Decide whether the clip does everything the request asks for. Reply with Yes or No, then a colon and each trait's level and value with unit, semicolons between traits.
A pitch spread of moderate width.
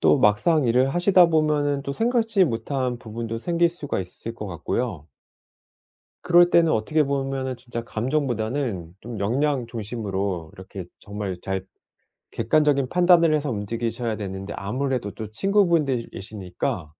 No: wide, 6.2 semitones